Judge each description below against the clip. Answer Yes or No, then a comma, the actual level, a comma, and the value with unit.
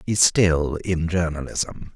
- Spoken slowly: Yes, slow, 125 wpm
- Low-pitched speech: Yes, very low, 85 Hz